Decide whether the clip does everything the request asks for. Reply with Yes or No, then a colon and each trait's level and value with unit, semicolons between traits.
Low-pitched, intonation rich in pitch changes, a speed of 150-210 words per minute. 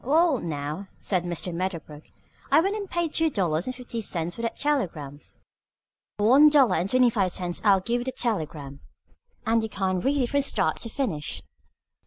No: high, 210 Hz; wide, 7.2 semitones; average, 190 wpm